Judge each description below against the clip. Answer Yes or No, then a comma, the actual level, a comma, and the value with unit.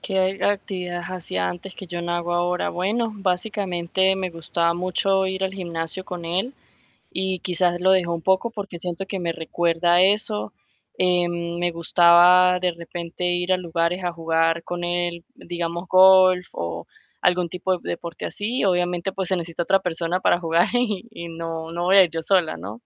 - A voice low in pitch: No, medium, 175 Hz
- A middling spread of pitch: No, narrow, 1.8 semitones